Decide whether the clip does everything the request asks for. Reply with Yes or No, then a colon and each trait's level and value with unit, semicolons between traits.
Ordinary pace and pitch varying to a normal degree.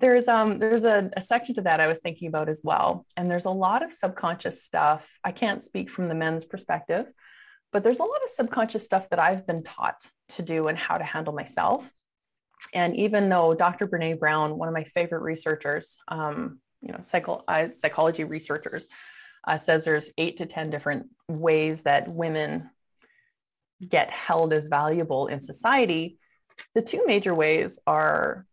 Yes: average, 180 wpm; average, 4.7 semitones